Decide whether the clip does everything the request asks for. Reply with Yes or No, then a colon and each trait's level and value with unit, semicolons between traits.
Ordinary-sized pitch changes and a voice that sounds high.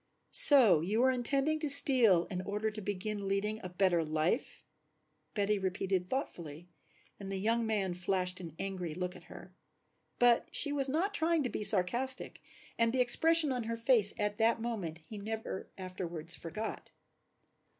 Yes: average, 5.0 semitones; high, 210 Hz